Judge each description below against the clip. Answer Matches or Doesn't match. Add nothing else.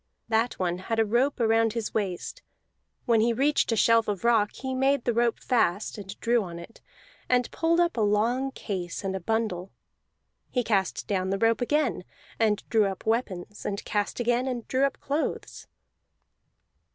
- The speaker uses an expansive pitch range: Doesn't match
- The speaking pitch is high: Matches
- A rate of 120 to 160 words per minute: Doesn't match